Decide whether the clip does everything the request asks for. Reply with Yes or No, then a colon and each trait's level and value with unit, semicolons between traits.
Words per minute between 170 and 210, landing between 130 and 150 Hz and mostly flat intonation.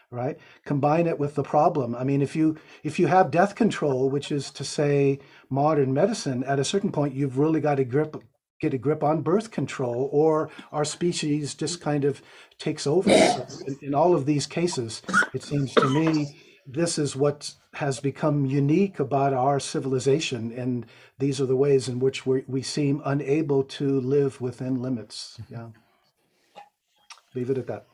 Yes: average, 180 wpm; medium, 140 Hz; narrow, 2.3 semitones